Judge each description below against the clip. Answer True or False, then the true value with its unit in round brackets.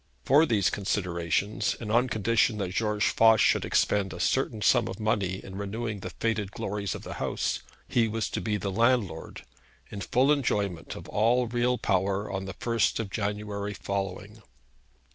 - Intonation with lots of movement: False (2.7 semitones)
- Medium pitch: False (105 Hz)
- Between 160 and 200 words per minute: True (170 wpm)